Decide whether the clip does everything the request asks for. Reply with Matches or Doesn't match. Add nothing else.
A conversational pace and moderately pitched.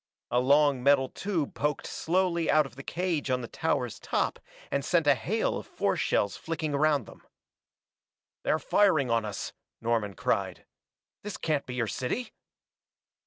Matches